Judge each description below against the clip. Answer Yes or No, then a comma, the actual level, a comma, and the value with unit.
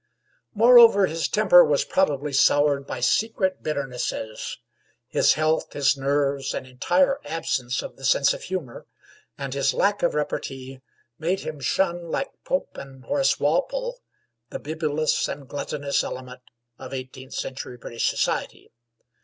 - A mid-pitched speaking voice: Yes, medium, 145 Hz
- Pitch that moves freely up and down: Yes, wide, 5.7 semitones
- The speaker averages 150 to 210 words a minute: No, slow, 135 wpm